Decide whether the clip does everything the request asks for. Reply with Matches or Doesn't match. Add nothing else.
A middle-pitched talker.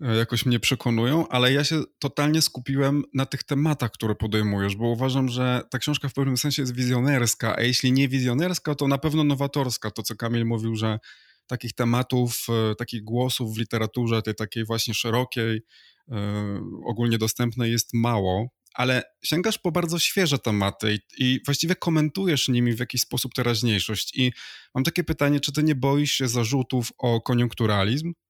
Doesn't match